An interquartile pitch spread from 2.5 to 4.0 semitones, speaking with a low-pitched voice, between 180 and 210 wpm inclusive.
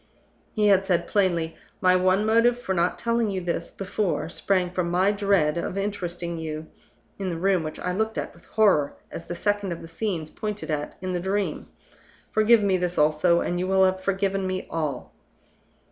No: average, 2.8 semitones; medium, 185 Hz; average, 190 wpm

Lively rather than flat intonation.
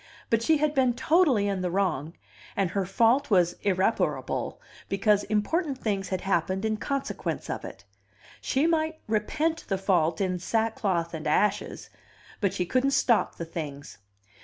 Yes: wide, 6.0 semitones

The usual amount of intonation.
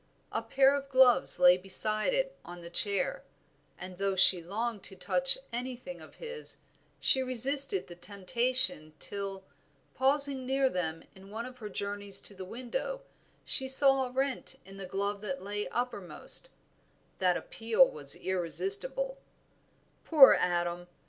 No: wide, 6.1 semitones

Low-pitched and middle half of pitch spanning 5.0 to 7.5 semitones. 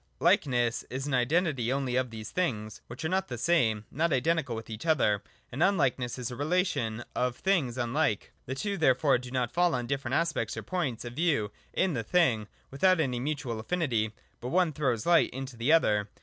Yes: low, 130 Hz; average, 5.3 semitones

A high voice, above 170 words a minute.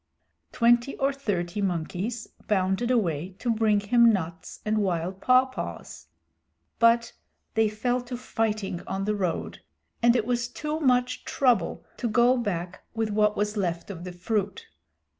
No: high, 215 Hz; average, 145 wpm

